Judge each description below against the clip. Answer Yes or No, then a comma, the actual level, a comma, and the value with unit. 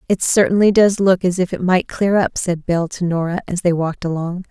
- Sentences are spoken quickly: Yes, fast, 240 wpm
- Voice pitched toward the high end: No, medium, 180 Hz